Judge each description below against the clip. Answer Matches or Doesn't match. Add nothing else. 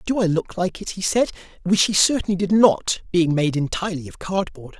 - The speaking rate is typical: Doesn't match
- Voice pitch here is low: Doesn't match